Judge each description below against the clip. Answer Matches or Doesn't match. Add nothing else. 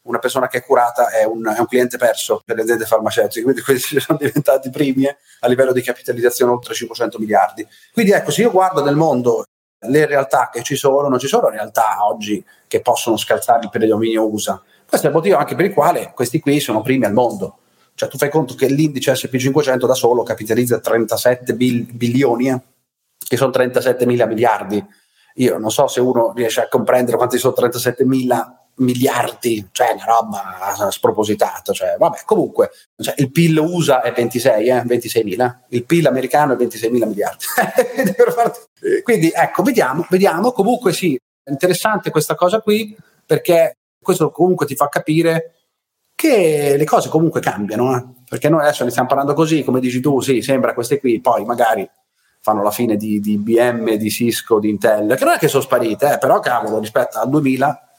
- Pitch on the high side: Doesn't match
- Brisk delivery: Matches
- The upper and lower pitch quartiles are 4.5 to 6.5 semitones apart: Matches